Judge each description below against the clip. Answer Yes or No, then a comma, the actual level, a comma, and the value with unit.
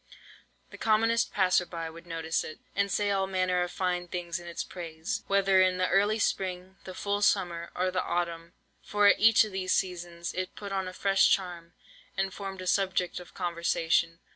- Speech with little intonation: Yes, narrow, 2.1 semitones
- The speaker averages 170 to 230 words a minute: Yes, average, 190 wpm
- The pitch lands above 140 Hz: Yes, medium, 185 Hz